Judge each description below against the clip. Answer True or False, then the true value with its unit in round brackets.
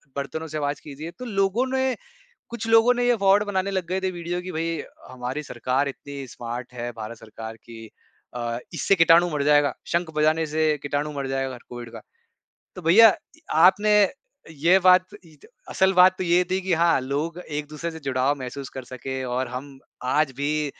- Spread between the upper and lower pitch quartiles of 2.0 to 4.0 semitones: False (5.4 semitones)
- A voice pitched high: False (155 Hz)